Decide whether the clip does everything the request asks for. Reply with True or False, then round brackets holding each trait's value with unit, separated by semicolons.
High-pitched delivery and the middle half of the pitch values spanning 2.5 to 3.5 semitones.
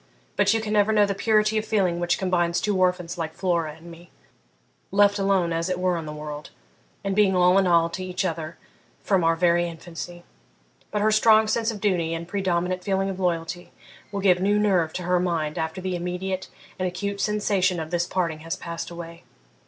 False (180 Hz; 2.8 semitones)